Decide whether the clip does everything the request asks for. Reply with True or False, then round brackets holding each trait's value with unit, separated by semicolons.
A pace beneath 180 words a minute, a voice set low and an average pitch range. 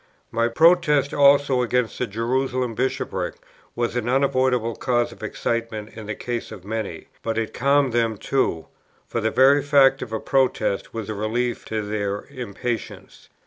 True (160 wpm; 120 Hz; 3.0 semitones)